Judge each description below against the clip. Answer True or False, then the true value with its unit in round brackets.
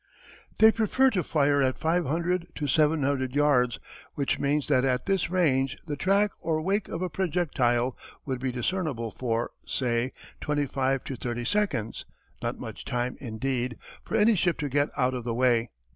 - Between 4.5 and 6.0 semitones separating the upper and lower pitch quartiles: True (5.2 semitones)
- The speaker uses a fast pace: False (170 wpm)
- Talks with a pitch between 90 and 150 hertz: True (140 Hz)